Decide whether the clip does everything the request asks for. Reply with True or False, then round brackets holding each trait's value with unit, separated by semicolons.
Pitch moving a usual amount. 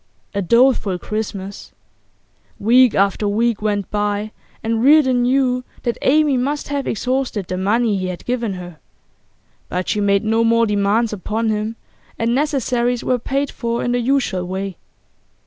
True (3.7 semitones)